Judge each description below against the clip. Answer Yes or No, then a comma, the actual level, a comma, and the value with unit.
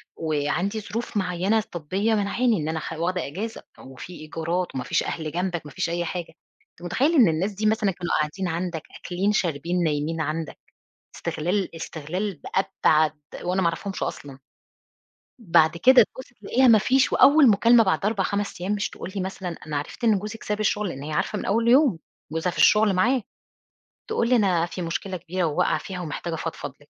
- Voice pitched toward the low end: No, medium, 185 Hz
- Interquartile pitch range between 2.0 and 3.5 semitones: No, average, 4.4 semitones